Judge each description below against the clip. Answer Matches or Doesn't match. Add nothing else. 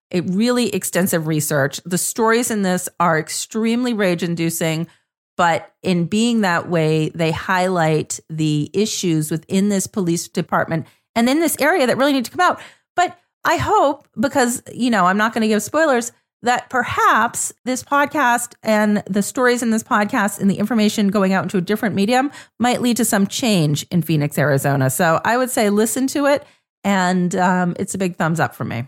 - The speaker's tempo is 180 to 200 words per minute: Matches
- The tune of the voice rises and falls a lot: Matches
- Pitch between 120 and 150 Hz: Doesn't match